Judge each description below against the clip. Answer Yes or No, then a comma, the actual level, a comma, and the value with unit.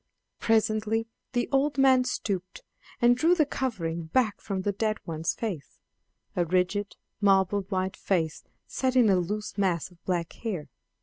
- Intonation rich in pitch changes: No, average, 4.6 semitones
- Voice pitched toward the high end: Yes, high, 205 Hz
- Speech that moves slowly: No, average, 150 wpm